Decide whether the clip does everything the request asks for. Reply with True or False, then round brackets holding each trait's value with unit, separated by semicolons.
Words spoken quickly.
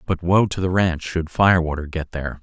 True (250 wpm)